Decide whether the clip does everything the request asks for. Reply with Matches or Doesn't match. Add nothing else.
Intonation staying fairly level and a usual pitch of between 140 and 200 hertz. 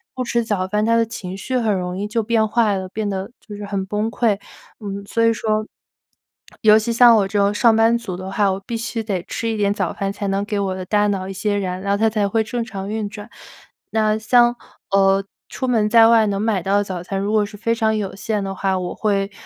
Doesn't match